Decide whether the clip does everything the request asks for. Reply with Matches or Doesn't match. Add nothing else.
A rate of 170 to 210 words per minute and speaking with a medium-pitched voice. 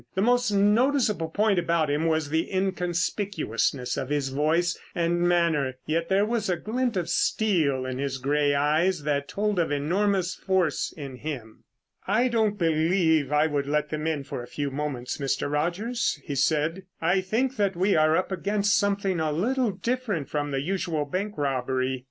Matches